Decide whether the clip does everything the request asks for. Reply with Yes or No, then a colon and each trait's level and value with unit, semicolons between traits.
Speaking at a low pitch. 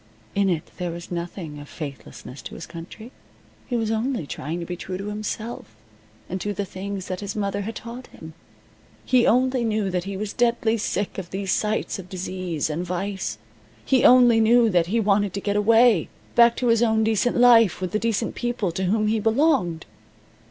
No: high, 205 Hz